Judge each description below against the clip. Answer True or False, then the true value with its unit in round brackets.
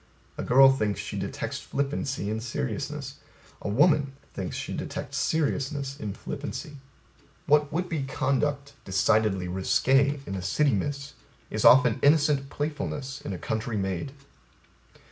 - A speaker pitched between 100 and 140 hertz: True (135 Hz)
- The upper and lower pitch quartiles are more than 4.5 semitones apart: True (5.1 semitones)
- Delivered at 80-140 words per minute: True (135 wpm)